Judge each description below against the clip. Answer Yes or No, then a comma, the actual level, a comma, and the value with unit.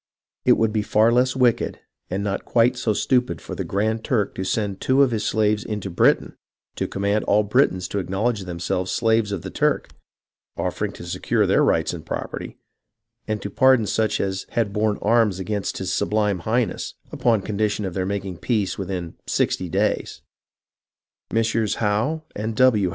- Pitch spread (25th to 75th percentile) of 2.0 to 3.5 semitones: Yes, average, 2.7 semitones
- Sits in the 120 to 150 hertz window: No, low, 105 Hz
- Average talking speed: Yes, average, 175 wpm